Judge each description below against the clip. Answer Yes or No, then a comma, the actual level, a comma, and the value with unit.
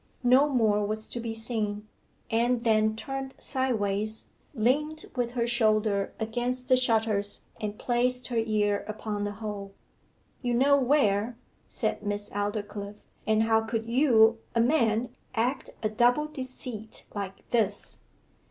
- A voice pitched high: Yes, high, 225 Hz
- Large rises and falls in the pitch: No, average, 2.9 semitones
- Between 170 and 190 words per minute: No, slow, 135 wpm